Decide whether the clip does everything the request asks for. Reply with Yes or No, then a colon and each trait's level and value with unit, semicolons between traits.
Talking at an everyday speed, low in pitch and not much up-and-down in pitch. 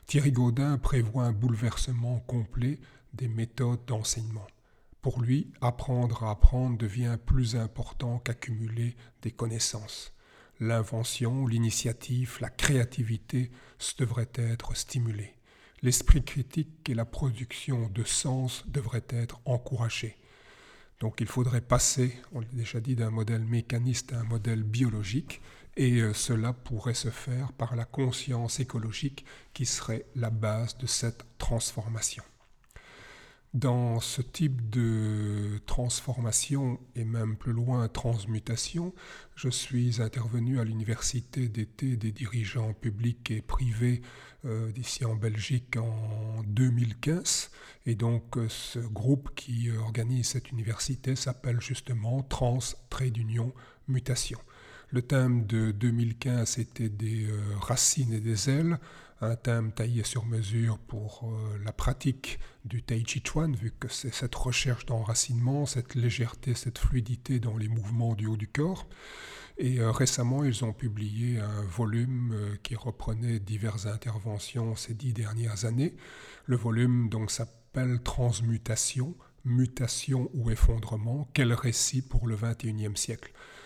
No: slow, 125 wpm; low, 120 Hz; narrow, 1.9 semitones